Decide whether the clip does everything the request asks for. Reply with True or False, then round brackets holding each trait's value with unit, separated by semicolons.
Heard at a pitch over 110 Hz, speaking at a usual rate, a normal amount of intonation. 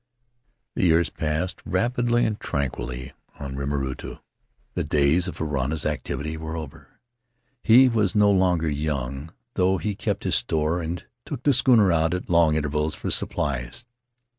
False (80 Hz; 150 wpm; 4.5 semitones)